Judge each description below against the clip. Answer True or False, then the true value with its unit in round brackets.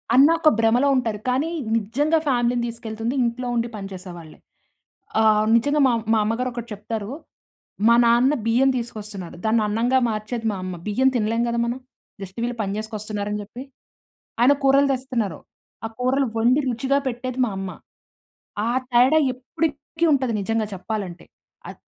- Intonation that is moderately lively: True (3.2 semitones)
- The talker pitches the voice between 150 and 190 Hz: False (235 Hz)